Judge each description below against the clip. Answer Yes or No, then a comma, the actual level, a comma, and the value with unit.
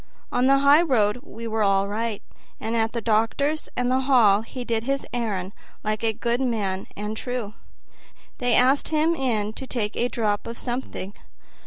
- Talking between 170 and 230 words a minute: Yes, average, 175 wpm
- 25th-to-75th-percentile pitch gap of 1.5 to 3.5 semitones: Yes, average, 3.2 semitones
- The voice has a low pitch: No, high, 230 Hz